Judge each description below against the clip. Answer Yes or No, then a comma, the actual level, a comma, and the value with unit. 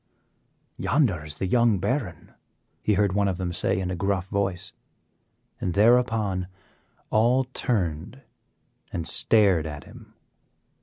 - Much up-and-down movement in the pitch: No, average, 3.8 semitones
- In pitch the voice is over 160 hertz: No, very low, 95 Hz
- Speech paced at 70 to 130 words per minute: Yes, slow, 125 wpm